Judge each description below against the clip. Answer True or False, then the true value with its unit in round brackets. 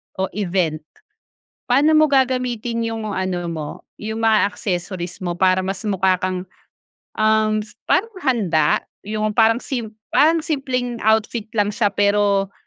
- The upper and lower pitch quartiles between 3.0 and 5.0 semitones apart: True (3.9 semitones)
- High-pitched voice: True (215 Hz)